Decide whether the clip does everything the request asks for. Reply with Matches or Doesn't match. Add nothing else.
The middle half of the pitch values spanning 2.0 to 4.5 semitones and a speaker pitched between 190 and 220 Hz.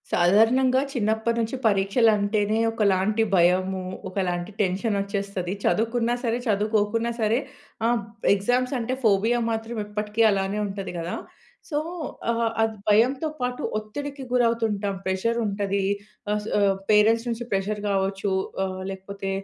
Matches